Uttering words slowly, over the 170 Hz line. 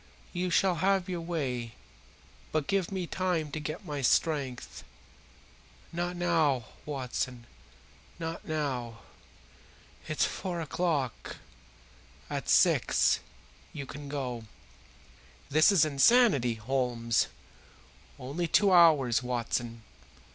No: slow, 100 wpm; medium, 150 Hz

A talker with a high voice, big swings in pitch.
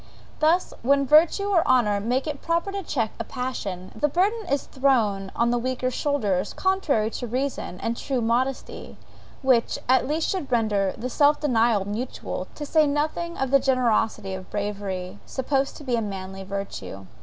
Yes: very high, 255 Hz; wide, 5.7 semitones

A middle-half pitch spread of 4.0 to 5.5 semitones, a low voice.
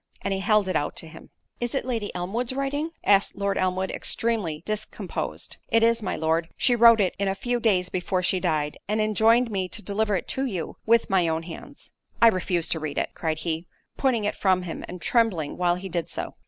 No: average, 4.4 semitones; high, 195 Hz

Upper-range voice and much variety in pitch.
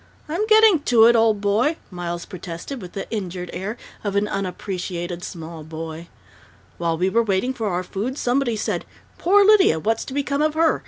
Yes: high, 205 Hz; wide, 6.8 semitones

